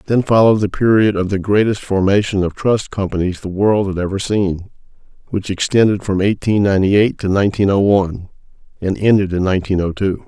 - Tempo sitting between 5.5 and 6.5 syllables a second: Yes, 5.8 syllables/s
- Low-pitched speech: Yes, low, 100 Hz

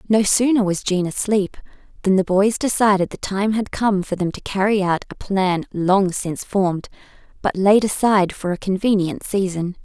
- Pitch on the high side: Yes, high, 195 Hz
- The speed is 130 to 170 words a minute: No, average, 185 wpm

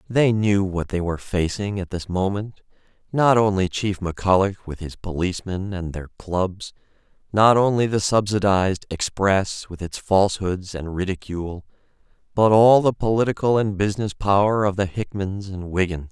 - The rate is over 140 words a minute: Yes, average, 155 wpm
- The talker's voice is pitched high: No, low, 100 Hz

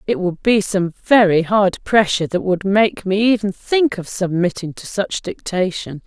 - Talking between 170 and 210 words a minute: Yes, average, 180 wpm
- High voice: Yes, high, 195 Hz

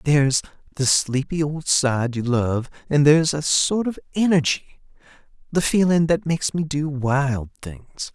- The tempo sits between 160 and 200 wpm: No, average, 145 wpm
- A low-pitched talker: No, medium, 145 Hz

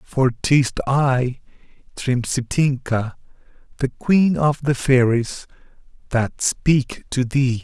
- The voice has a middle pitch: No, low, 130 Hz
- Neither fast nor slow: No, slow, 100 wpm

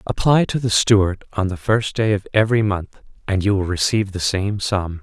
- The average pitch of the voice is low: Yes, low, 100 Hz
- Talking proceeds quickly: Yes, fast, 215 wpm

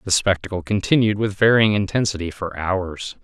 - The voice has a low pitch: Yes, low, 100 Hz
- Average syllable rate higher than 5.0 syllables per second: Yes, 5.2 syllables/s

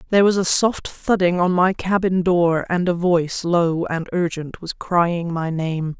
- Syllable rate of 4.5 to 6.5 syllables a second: No, 4.2 syllables/s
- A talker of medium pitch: Yes, medium, 175 Hz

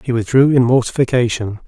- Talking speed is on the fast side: No, average, 145 wpm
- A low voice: Yes, low, 120 Hz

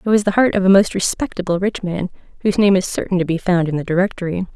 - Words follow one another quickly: Yes, fast, 265 wpm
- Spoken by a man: No, female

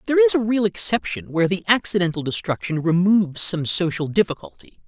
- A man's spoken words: Yes, male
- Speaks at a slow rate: No, average, 160 wpm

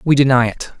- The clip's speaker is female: No, male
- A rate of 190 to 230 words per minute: Yes, fast, 225 wpm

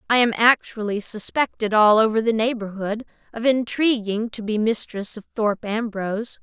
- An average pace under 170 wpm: Yes, average, 150 wpm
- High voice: Yes, high, 220 Hz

